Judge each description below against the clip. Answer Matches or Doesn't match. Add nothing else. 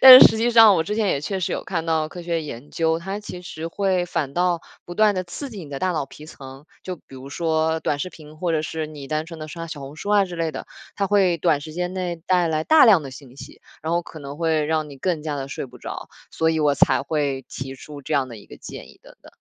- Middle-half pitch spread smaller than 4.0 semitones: Matches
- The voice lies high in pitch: Doesn't match